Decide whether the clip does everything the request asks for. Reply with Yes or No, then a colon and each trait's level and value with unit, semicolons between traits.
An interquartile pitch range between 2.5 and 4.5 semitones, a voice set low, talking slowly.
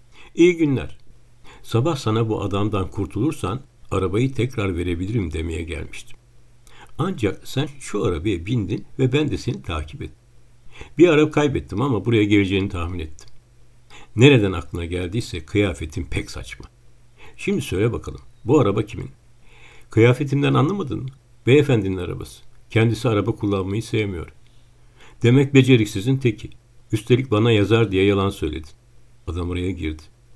No: average, 3.6 semitones; low, 115 Hz; average, 125 wpm